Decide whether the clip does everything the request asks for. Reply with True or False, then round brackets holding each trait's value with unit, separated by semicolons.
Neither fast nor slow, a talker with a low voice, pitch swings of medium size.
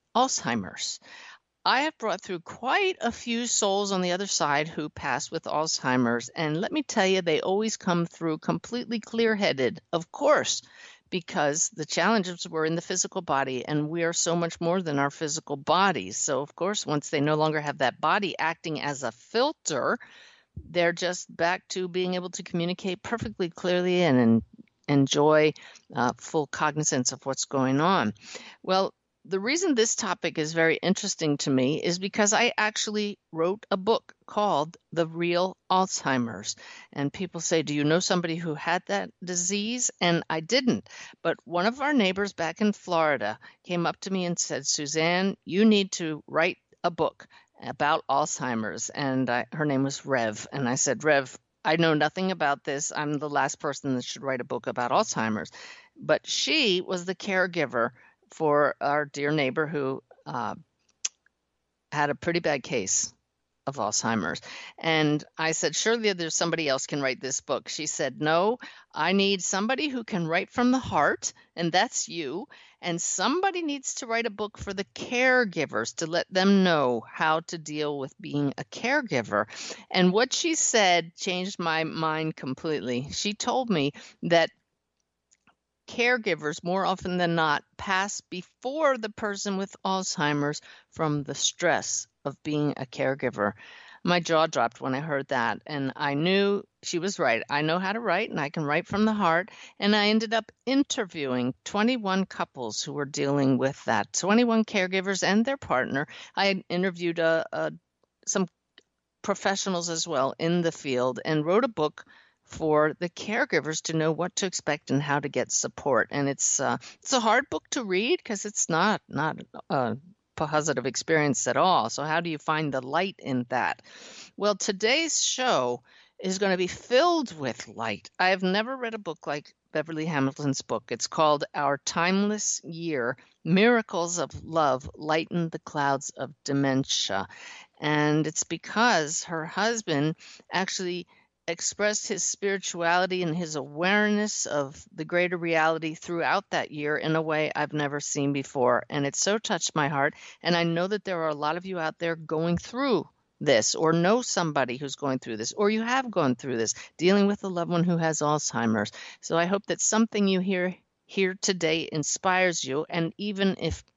False (175 wpm; 170 Hz; 5.0 semitones)